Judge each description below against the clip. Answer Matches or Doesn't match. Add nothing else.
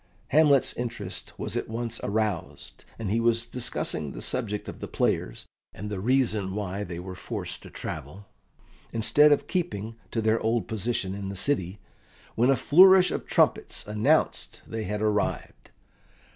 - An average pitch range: Matches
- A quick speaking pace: Doesn't match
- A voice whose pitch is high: Doesn't match